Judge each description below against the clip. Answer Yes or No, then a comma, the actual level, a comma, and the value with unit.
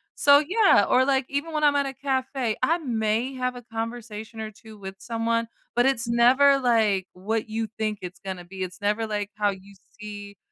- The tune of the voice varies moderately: Yes, average, 3.9 semitones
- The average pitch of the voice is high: Yes, high, 225 Hz